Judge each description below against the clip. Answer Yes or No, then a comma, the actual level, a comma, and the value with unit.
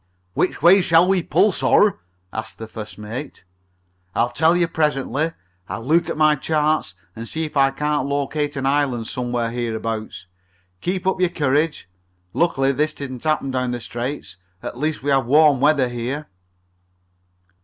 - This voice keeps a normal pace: Yes, average, 165 wpm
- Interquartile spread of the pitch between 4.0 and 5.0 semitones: Yes, average, 4.4 semitones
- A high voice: No, medium, 140 Hz